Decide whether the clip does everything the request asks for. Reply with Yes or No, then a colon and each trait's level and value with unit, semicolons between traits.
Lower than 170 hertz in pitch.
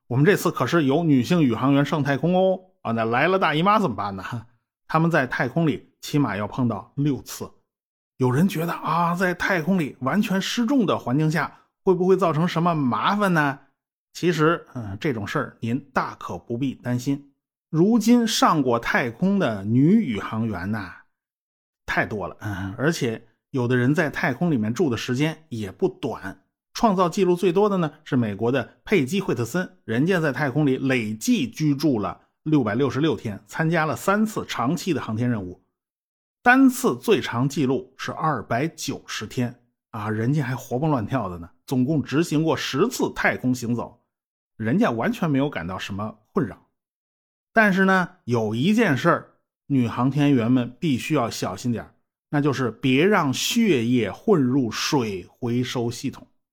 Yes: medium, 140 Hz